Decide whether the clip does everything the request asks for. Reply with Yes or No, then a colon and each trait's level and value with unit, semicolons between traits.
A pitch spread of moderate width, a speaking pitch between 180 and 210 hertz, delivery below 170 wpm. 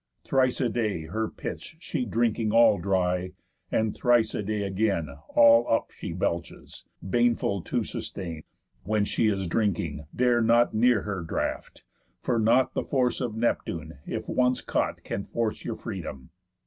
No: average, 4.2 semitones; low, 110 Hz; average, 155 wpm